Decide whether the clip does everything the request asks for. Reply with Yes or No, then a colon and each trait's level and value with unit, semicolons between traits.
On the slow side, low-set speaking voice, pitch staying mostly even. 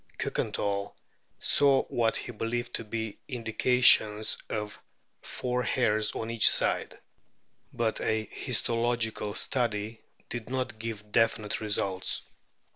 Yes: slow, 115 wpm; low, 115 Hz; narrow, 2.1 semitones